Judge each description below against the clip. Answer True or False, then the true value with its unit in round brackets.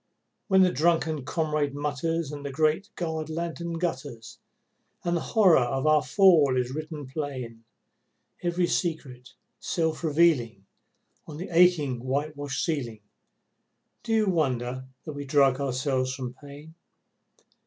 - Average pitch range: True (4.0 semitones)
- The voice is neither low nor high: True (150 Hz)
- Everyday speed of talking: False (130 wpm)